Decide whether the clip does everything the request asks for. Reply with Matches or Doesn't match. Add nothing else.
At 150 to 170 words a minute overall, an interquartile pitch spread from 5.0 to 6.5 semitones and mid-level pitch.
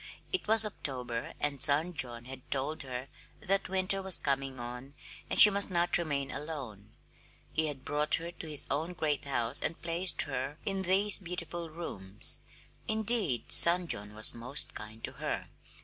Matches